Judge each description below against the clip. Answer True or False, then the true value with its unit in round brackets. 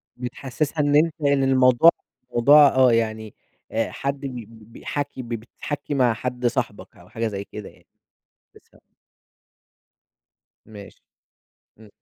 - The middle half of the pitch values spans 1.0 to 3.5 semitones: False (3.9 semitones)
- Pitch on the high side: False (125 Hz)